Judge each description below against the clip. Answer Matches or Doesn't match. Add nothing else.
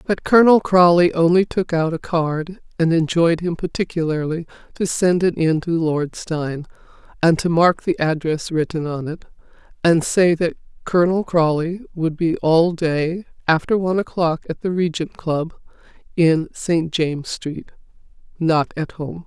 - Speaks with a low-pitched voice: Doesn't match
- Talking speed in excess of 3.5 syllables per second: Matches